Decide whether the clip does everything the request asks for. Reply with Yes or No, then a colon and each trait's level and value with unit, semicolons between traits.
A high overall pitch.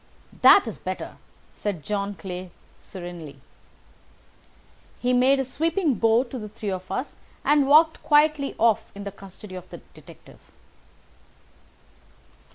Yes: high, 220 Hz